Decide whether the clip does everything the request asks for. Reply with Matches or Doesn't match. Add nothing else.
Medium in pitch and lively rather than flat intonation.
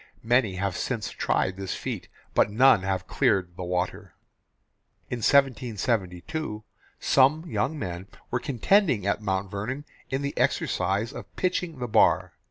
Doesn't match